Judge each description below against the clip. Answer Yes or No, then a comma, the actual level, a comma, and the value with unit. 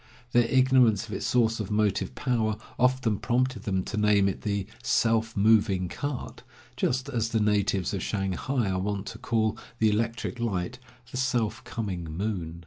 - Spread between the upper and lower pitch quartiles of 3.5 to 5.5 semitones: No, average, 3.0 semitones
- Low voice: Yes, low, 110 Hz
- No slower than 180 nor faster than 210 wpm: No, average, 165 wpm